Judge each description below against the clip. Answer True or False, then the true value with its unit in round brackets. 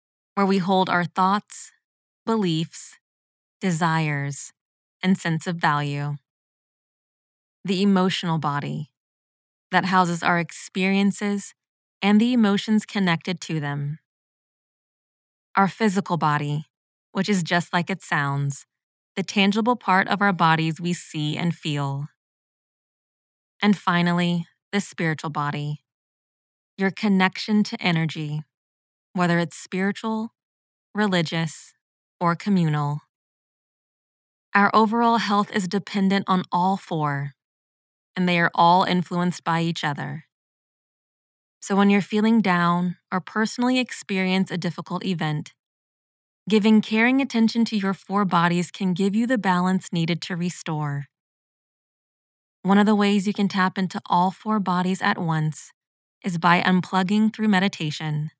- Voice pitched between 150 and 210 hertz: True (185 Hz)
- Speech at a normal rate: False (120 wpm)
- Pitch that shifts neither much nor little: True (3.9 semitones)